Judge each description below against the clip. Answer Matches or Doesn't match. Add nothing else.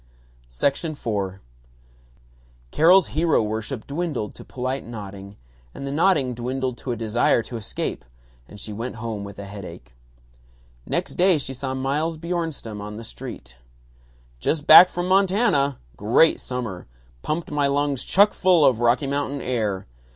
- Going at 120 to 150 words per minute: Matches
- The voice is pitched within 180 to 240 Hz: Doesn't match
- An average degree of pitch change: Doesn't match